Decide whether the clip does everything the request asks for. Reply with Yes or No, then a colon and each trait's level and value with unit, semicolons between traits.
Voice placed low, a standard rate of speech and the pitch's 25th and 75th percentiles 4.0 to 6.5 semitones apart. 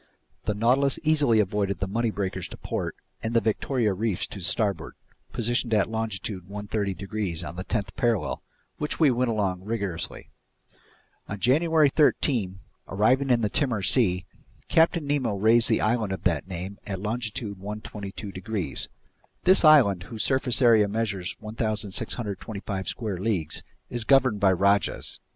No: low, 105 Hz; average, 145 wpm; average, 3.5 semitones